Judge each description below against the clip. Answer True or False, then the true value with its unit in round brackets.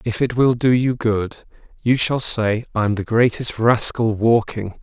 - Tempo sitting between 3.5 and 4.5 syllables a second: True (4.0 syllables/s)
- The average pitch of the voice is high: False (115 Hz)